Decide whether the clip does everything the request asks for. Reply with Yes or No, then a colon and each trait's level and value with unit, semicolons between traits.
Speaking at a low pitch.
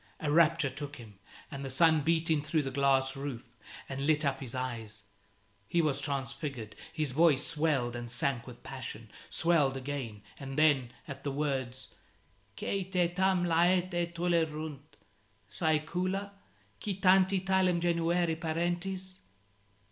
No: medium, 150 Hz